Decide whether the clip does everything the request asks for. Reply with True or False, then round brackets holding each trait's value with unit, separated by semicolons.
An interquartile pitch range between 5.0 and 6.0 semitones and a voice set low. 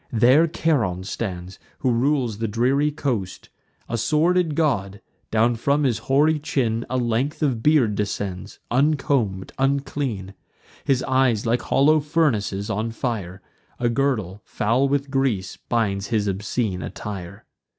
True (5.3 semitones; 120 Hz)